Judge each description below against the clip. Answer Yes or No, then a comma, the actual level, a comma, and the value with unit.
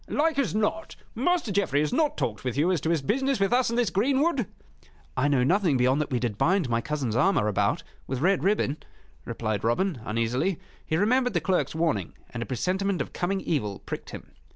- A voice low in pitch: No, medium, 170 Hz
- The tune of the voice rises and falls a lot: Yes, wide, 8.7 semitones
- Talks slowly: No, fast, 205 wpm